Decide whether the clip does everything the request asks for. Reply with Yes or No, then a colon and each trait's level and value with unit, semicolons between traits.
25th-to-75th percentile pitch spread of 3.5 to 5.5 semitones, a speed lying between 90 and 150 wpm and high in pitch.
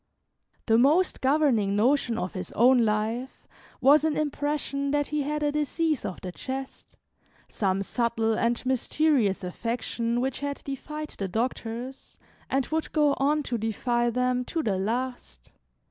Yes: average, 4.4 semitones; average, 145 wpm; very high, 255 Hz